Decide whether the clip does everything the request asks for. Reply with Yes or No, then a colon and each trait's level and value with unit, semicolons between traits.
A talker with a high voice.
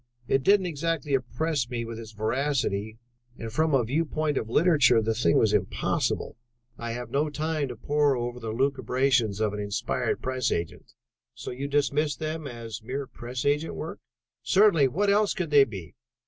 No: low, 130 Hz